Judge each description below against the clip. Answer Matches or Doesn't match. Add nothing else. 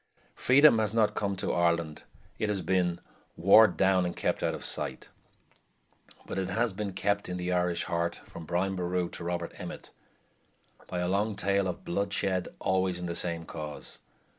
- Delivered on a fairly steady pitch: Matches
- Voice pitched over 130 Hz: Doesn't match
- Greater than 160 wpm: Matches